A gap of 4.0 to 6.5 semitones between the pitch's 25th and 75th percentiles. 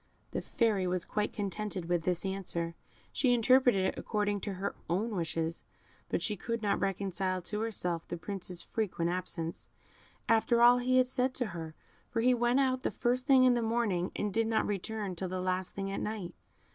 Yes: average, 4.3 semitones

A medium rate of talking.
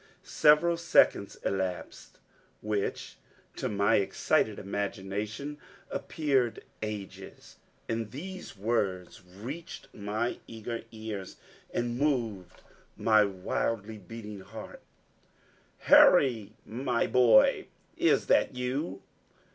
No: slow, 90 wpm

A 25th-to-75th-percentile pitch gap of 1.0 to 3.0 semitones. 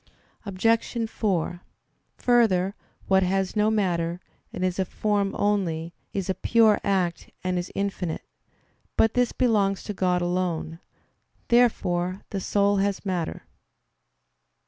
Yes: average, 2.7 semitones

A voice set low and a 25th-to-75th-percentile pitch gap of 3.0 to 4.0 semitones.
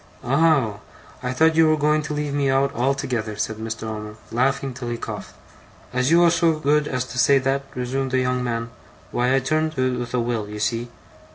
Yes: low, 130 Hz; average, 3.4 semitones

